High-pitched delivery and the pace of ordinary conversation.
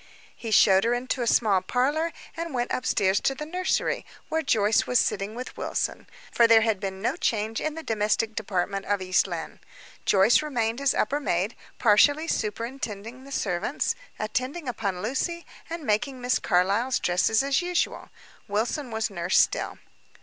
Yes: high, 230 Hz; average, 165 wpm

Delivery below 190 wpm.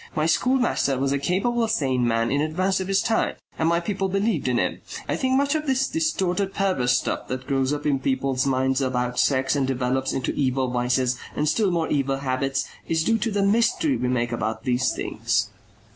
No: fast, 205 wpm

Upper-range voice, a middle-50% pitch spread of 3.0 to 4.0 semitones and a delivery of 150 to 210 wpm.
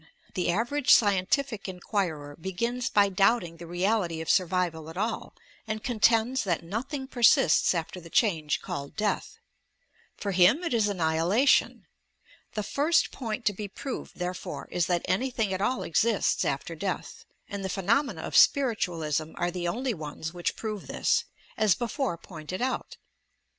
No: high, 195 Hz; average, 5.1 semitones; average, 155 wpm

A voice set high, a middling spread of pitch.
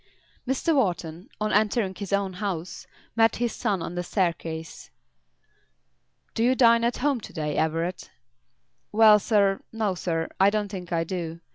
Yes: high, 195 Hz; average, 4.5 semitones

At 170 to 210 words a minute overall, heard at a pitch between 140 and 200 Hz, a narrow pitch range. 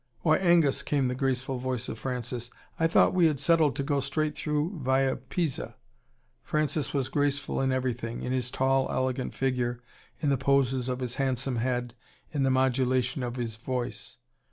No: average, 175 wpm; low, 130 Hz; narrow, 2.2 semitones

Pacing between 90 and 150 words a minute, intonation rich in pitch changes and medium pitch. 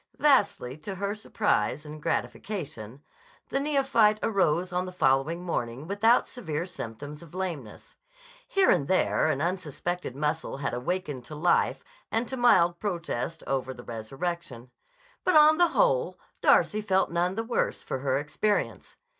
Yes: average, 145 wpm; wide, 6.9 semitones; medium, 175 Hz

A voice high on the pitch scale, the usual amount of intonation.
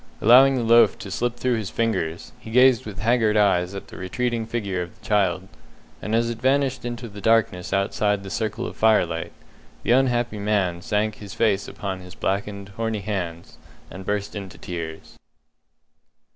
No: low, 105 Hz; average, 3.4 semitones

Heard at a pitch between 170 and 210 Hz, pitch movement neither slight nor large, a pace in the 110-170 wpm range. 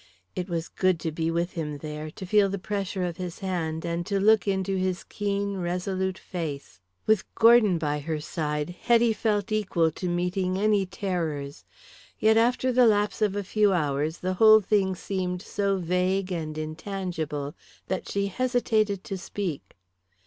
Yes: medium, 185 Hz; average, 3.5 semitones; average, 165 wpm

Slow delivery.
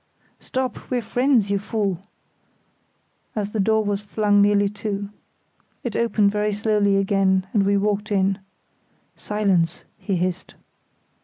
Yes: slow, 130 wpm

